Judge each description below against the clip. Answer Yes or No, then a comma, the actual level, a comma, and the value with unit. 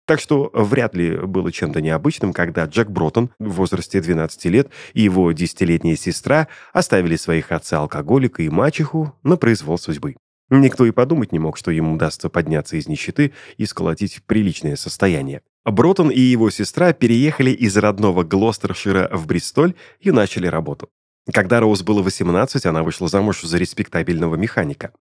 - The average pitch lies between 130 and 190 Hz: No, low, 100 Hz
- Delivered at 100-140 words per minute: No, average, 155 wpm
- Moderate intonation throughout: No, wide, 6.4 semitones